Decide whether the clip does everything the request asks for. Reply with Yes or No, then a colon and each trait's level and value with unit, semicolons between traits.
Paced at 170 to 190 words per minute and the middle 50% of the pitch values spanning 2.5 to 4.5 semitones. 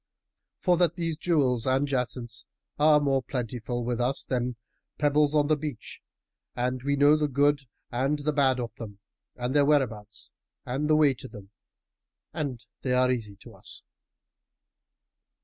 No: average, 155 wpm; average, 3.3 semitones